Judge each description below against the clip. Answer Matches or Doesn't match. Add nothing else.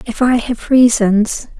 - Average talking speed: Matches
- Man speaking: Doesn't match